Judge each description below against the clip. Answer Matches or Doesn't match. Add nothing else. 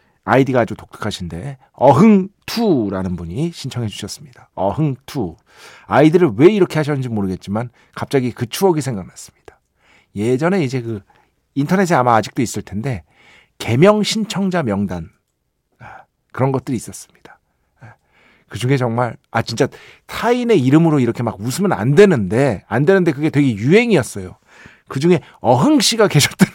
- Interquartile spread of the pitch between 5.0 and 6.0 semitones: Doesn't match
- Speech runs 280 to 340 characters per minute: Matches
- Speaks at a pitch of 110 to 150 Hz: Matches